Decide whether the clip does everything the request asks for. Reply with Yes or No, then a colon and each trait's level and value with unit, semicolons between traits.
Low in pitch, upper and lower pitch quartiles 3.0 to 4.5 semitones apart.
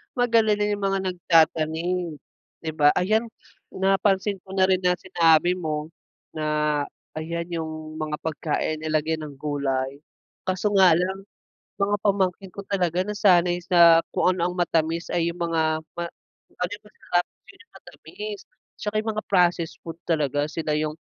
No: medium, 170 Hz; average, 3.3 semitones